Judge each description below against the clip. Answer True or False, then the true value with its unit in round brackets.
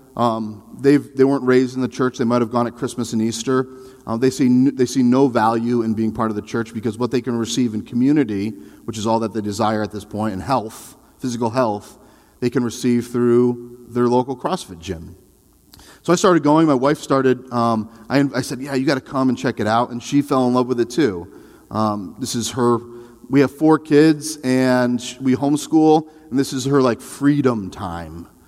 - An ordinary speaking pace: False (215 wpm)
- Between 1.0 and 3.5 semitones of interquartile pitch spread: True (2.8 semitones)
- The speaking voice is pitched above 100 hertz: True (125 Hz)